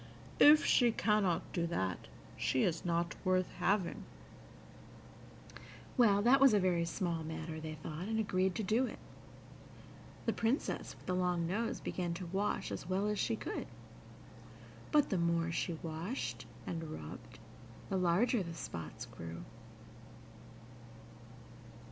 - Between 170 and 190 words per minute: No, slow, 135 wpm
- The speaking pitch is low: No, medium, 180 Hz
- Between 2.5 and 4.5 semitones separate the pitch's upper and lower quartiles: Yes, average, 4.0 semitones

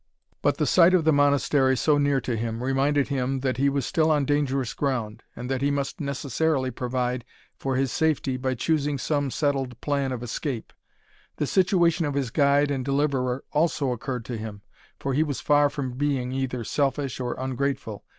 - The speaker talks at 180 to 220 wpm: Yes, average, 185 wpm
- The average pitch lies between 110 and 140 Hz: Yes, low, 135 Hz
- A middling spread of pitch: No, narrow, 2.3 semitones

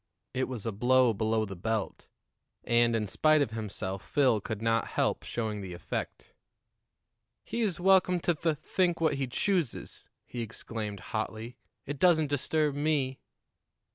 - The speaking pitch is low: Yes, low, 125 Hz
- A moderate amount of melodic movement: No, wide, 5.9 semitones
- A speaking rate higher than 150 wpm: No, average, 145 wpm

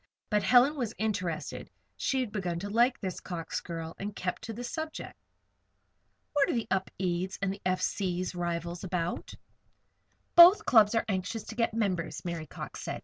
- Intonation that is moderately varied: Yes, average, 4.4 semitones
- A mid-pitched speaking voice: No, high, 195 Hz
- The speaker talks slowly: No, average, 170 wpm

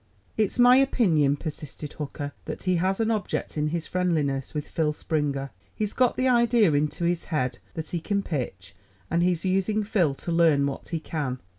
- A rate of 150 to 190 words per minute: Yes, average, 185 wpm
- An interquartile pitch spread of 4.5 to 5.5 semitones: Yes, average, 5.1 semitones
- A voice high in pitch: No, medium, 165 Hz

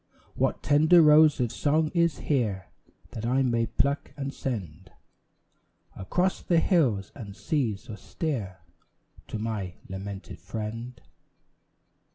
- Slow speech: Yes, slow, 115 wpm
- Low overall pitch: Yes, low, 120 Hz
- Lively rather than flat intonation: Yes, wide, 6.5 semitones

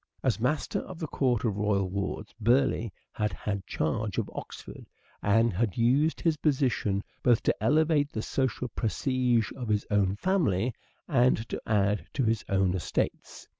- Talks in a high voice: No, low, 115 Hz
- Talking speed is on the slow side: No, average, 160 wpm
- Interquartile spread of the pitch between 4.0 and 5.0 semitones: Yes, average, 4.5 semitones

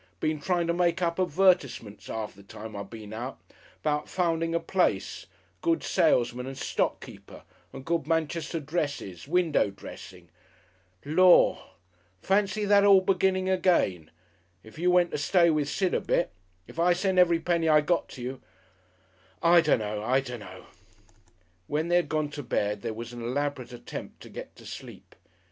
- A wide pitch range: Yes, wide, 6.5 semitones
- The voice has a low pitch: No, medium, 155 Hz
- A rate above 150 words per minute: Yes, average, 165 wpm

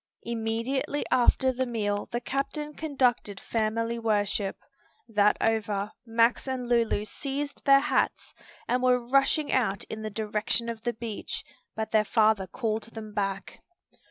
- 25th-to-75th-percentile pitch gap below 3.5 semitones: Yes, average, 2.9 semitones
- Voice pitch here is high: Yes, high, 230 Hz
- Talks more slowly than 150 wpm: Yes, average, 140 wpm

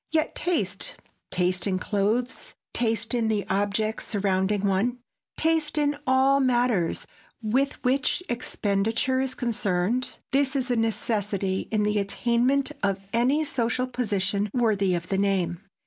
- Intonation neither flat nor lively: Yes, average, 4.3 semitones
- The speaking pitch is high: Yes, high, 225 Hz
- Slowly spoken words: Yes, slow, 125 wpm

